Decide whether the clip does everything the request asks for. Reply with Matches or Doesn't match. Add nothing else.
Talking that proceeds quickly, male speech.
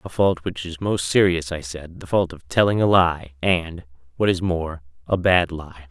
Matches